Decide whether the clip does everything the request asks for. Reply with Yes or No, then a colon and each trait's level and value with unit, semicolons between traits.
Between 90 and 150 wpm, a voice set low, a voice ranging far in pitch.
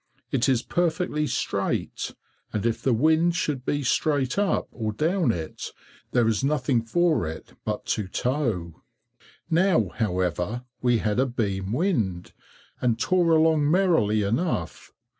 Yes: average, 140 wpm; low, 125 Hz; wide, 6.9 semitones